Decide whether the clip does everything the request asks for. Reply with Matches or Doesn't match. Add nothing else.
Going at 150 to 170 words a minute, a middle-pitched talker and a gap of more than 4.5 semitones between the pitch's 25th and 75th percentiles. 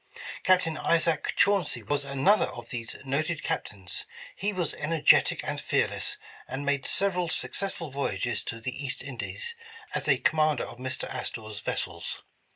Matches